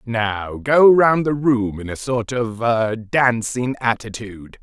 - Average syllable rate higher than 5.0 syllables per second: No, 3.6 syllables/s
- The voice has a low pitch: Yes, low, 120 Hz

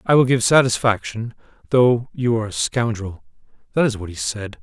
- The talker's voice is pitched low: Yes, low, 110 Hz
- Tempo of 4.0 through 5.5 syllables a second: Yes, 5.0 syllables/s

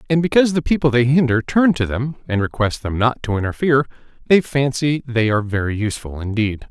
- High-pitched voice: No, low, 125 Hz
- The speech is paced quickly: No, average, 195 wpm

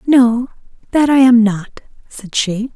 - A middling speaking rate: Yes, average, 155 wpm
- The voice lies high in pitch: Yes, high, 240 Hz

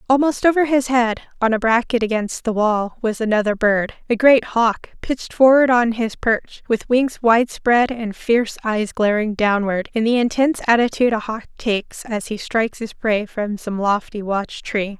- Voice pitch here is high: Yes, high, 225 Hz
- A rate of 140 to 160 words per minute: No, average, 190 wpm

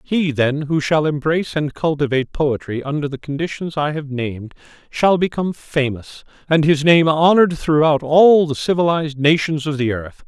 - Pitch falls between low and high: Yes, medium, 150 Hz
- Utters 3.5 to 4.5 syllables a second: No, 5.1 syllables/s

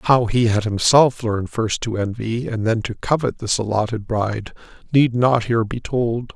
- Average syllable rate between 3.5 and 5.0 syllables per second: Yes, 4.8 syllables/s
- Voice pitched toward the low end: Yes, low, 115 Hz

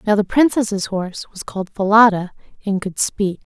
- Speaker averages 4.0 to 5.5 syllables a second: Yes, 5.1 syllables/s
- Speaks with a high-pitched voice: Yes, high, 200 Hz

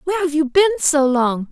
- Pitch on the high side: Yes, very high, 305 Hz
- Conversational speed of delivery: No, fast, 240 wpm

